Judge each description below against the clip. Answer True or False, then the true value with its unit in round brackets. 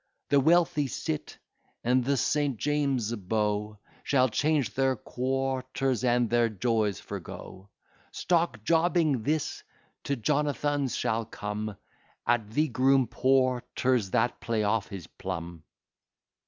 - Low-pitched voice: True (125 Hz)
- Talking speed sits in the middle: False (115 wpm)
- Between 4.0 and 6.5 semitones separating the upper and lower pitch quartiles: True (4.5 semitones)